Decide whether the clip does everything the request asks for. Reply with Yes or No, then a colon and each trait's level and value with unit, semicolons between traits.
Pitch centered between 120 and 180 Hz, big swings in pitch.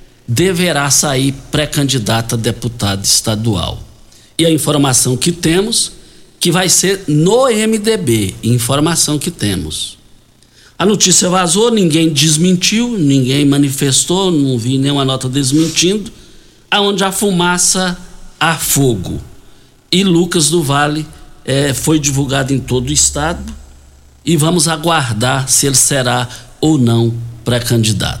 Yes: medium, 140 Hz; wide, 6.3 semitones